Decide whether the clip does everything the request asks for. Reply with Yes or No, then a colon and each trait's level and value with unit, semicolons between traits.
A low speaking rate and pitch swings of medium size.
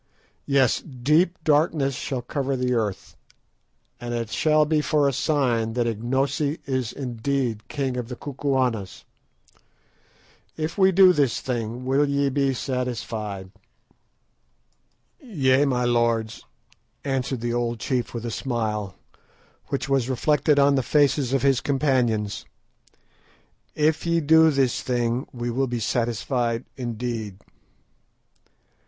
Yes: slow, 125 wpm; average, 3.2 semitones